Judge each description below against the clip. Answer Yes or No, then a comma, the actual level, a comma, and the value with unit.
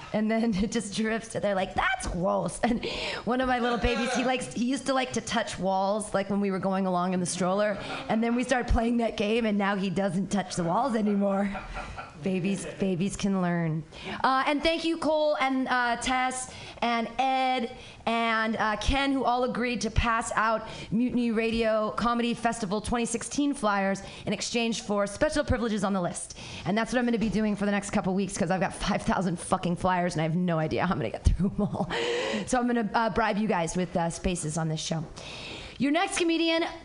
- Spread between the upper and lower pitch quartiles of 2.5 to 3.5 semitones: No, average, 3.9 semitones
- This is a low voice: No, high, 215 Hz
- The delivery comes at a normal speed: No, fast, 220 wpm